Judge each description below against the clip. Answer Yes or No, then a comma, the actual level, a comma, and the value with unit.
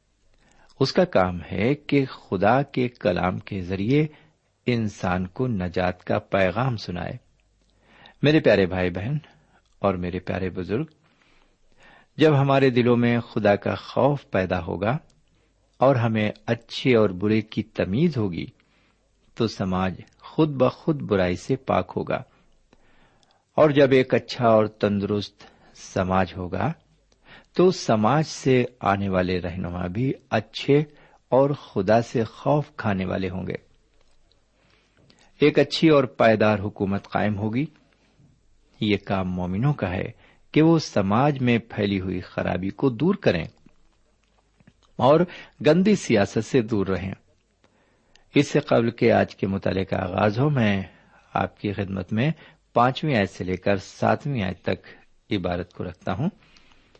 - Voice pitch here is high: No, low, 110 Hz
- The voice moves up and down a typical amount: No, wide, 6.1 semitones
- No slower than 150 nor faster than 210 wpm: No, average, 135 wpm